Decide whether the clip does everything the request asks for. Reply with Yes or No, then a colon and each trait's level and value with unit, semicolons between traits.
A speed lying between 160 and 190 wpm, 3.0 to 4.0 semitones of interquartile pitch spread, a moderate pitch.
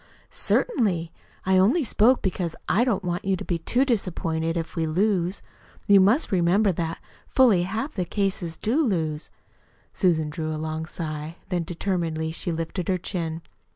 Yes: average, 170 wpm; average, 3.6 semitones; medium, 180 Hz